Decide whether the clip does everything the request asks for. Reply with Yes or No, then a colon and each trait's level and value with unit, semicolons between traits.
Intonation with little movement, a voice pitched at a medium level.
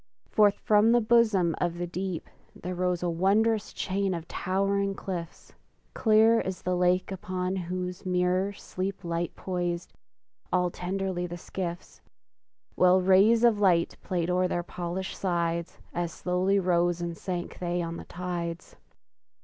Yes: narrow, 1.9 semitones; medium, 180 Hz